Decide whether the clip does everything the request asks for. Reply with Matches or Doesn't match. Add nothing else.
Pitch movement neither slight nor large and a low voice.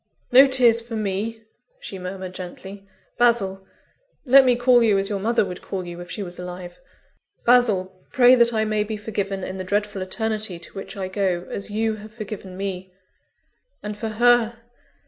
Doesn't match